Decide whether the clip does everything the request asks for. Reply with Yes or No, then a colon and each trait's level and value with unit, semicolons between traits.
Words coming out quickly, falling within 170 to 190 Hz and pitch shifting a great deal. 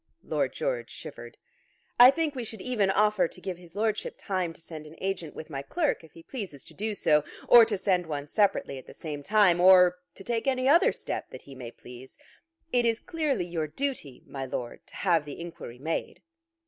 Yes: fast, 210 wpm; medium, 185 Hz; wide, 6.6 semitones